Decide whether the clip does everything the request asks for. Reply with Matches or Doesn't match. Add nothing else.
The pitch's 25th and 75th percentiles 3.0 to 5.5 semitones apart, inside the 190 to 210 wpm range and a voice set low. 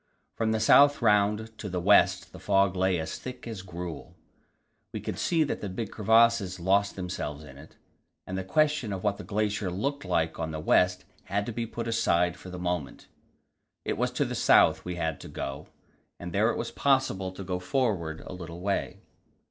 Matches